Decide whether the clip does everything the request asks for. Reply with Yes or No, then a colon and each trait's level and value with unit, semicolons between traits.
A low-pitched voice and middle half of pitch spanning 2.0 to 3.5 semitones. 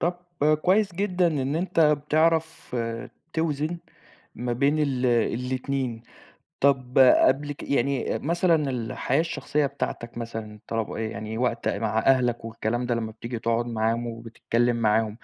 No: low, 125 Hz; average, 4.5 semitones